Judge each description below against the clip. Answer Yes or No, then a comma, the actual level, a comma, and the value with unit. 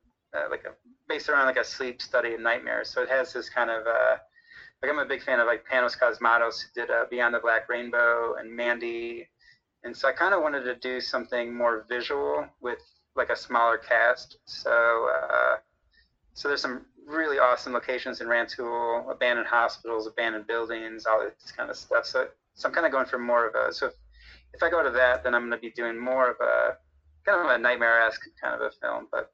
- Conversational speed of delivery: No, fast, 215 wpm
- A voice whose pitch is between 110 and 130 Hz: Yes, low, 120 Hz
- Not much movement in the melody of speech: Yes, narrow, 1.7 semitones